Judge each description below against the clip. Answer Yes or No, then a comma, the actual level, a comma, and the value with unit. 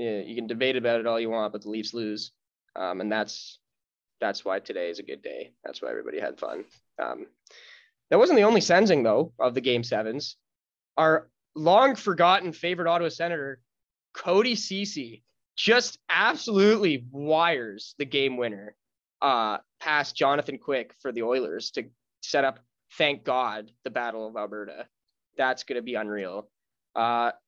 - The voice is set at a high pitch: No, medium, 140 Hz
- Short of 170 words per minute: Yes, average, 160 wpm